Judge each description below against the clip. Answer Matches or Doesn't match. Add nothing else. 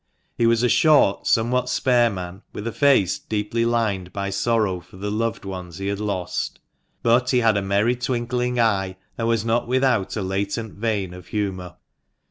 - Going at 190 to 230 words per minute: Doesn't match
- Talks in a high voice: Doesn't match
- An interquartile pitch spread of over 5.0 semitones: Doesn't match